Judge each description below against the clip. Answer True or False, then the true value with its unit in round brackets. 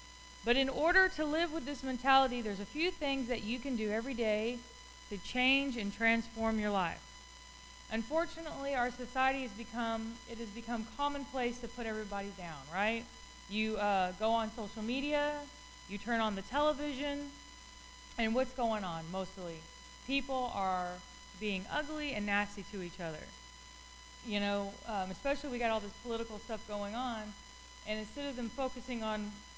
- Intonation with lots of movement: False (4.5 semitones)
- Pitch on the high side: True (225 Hz)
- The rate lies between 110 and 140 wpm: False (160 wpm)